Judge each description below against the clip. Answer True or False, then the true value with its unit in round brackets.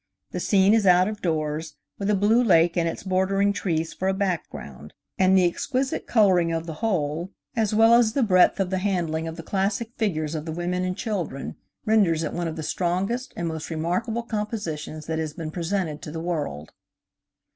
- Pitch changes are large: False (4.0 semitones)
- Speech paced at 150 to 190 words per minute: False (200 wpm)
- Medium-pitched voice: True (180 Hz)